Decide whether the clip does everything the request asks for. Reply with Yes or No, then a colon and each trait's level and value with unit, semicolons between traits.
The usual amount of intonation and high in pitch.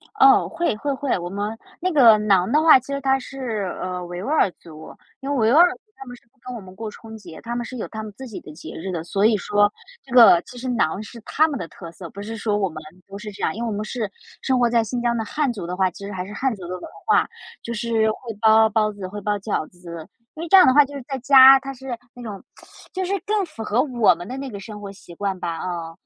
Yes: average, 4.9 semitones; high, 220 Hz